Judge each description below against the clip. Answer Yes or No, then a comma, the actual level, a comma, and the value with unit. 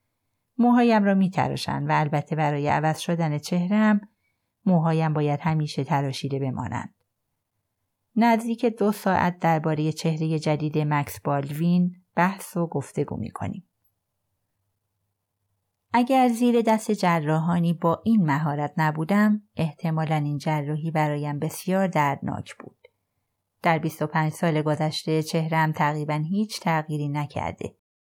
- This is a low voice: No, medium, 155 Hz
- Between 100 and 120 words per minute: Yes, slow, 105 wpm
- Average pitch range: Yes, average, 3.6 semitones